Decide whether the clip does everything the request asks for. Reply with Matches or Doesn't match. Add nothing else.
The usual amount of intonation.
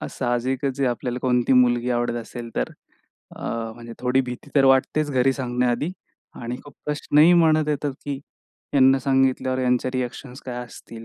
Doesn't match